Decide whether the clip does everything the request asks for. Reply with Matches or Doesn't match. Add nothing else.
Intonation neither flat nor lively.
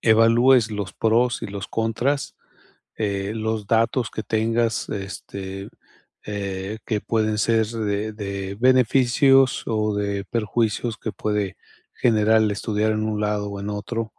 Doesn't match